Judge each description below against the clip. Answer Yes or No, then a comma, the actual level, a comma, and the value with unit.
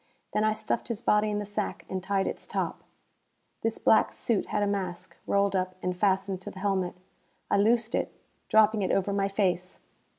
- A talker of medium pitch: No, high, 200 Hz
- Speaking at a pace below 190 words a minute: No, average, 195 wpm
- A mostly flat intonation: Yes, narrow, 2.0 semitones